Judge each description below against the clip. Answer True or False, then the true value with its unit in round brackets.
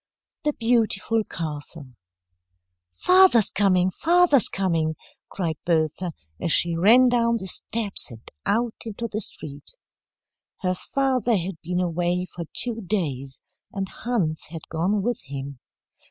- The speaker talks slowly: True (125 wpm)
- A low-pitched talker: False (185 Hz)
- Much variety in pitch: True (6.0 semitones)